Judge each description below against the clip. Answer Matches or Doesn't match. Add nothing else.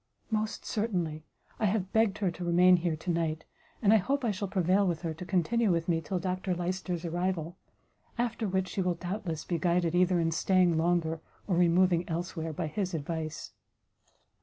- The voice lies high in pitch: Doesn't match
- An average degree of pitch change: Doesn't match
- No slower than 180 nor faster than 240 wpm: Matches